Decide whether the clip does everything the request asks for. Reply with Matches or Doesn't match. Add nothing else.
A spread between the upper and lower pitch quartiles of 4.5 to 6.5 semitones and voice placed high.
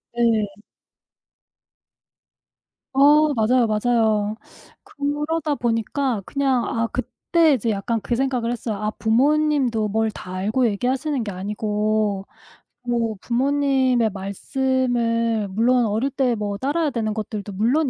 Doesn't match